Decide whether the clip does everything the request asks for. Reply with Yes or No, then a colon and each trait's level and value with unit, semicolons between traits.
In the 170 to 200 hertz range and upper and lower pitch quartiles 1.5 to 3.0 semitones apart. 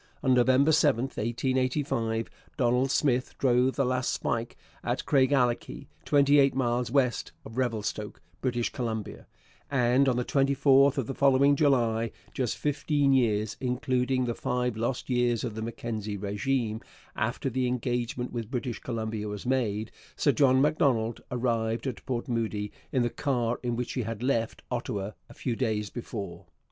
No: low, 125 Hz; narrow, 2.6 semitones